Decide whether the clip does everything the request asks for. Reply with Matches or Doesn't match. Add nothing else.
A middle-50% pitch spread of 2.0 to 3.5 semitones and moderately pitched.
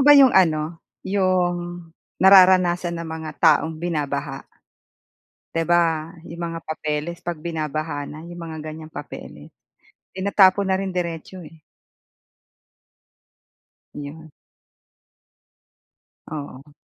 Matches